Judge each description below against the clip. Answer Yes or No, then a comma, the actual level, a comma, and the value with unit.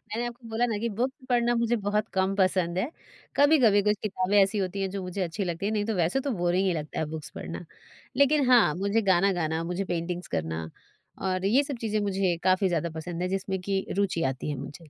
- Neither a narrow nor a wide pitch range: Yes, average, 3.9 semitones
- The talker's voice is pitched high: Yes, high, 195 Hz